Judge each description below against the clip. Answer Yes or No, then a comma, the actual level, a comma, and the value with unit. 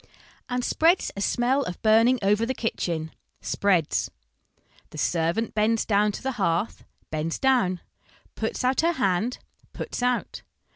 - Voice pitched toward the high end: Yes, high, 220 Hz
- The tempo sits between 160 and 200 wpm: No, average, 140 wpm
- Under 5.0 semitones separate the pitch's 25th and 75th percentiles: No, average, 5.3 semitones